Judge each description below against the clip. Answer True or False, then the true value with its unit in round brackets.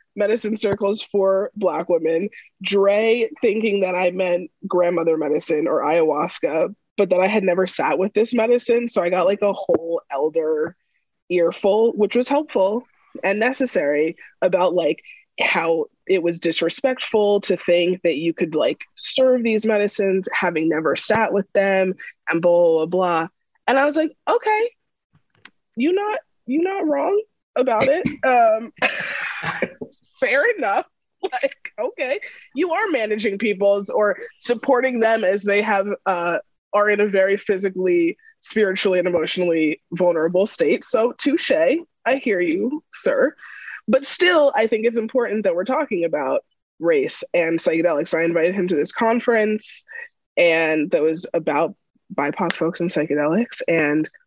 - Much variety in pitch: True (6.6 semitones)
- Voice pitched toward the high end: True (205 Hz)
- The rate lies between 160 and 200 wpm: False (145 wpm)